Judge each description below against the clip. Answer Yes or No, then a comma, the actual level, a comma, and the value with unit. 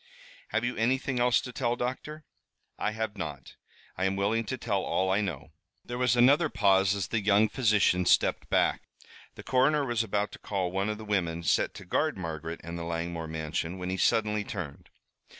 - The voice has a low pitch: Yes, low, 105 Hz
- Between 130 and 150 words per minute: No, average, 195 wpm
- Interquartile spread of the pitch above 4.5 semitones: Yes, average, 5.1 semitones